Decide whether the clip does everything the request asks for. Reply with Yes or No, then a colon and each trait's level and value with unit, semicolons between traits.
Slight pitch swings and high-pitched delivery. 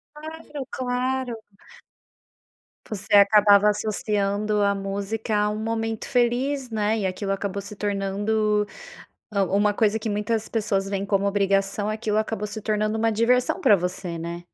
Yes: narrow, 1.9 semitones; high, 210 Hz